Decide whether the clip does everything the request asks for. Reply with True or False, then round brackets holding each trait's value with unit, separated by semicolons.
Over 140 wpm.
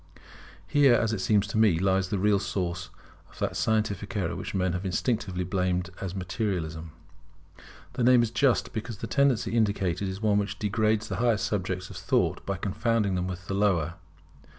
True (180 wpm)